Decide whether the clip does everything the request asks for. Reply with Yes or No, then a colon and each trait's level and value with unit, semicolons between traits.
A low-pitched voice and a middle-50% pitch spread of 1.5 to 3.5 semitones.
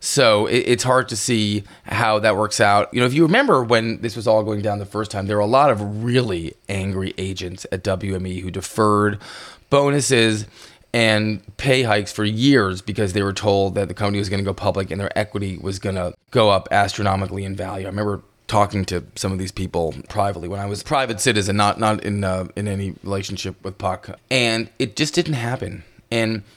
Yes: low, 105 Hz; narrow, 2.6 semitones